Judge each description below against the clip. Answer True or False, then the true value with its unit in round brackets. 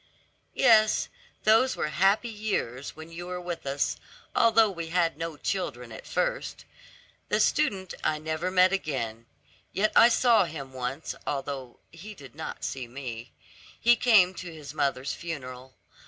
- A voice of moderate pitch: True (165 Hz)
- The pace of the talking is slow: False (150 wpm)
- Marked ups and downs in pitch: True (6.5 semitones)